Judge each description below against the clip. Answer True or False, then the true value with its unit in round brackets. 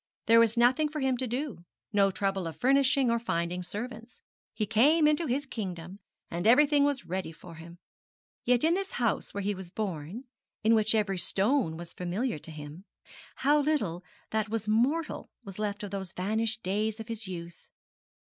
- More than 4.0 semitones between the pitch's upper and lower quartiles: True (5.4 semitones)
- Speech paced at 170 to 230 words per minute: True (180 wpm)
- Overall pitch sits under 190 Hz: False (215 Hz)